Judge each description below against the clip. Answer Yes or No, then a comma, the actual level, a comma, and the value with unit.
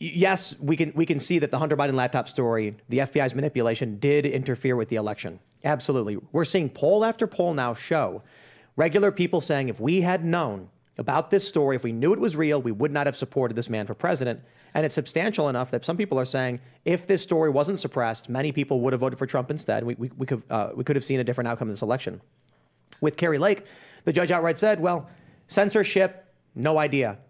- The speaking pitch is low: No, medium, 145 Hz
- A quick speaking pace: Yes, fast, 220 wpm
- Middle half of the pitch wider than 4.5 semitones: Yes, average, 5.0 semitones